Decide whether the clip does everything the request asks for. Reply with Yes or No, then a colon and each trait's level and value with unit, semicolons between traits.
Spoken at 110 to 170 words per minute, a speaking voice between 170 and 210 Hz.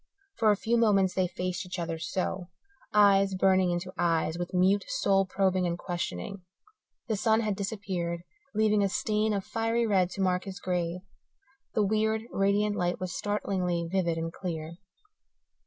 Yes: average, 160 wpm; high, 190 Hz